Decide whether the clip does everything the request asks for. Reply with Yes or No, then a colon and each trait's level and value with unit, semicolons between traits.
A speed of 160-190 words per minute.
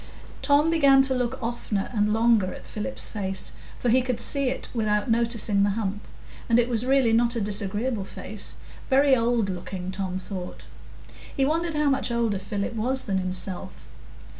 Yes: average, 165 wpm